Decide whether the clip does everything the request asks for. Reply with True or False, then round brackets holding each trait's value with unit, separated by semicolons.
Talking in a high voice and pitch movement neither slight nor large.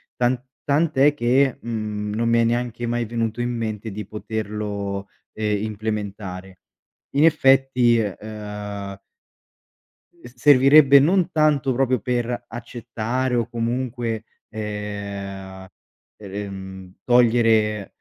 False (115 Hz; 3.0 semitones)